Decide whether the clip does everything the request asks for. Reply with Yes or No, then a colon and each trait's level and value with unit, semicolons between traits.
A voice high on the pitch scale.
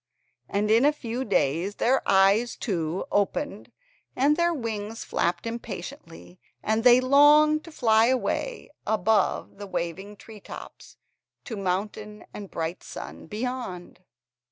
Yes: high, 220 Hz